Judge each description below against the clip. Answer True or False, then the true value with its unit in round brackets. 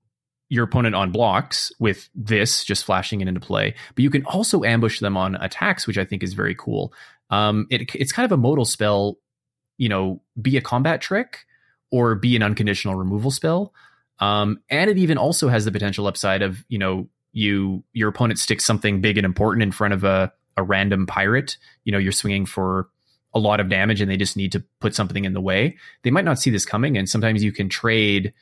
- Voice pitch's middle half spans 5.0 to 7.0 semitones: False (3.8 semitones)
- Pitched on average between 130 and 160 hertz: False (105 Hz)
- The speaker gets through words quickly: True (215 wpm)